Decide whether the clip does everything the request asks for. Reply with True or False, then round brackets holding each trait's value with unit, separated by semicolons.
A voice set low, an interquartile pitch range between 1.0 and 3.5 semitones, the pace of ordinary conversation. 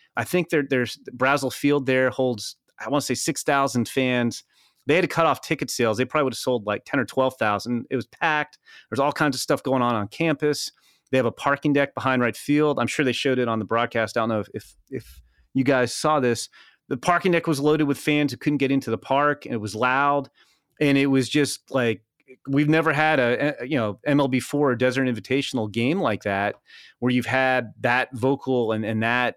False (130 Hz; 3.2 semitones; 235 wpm)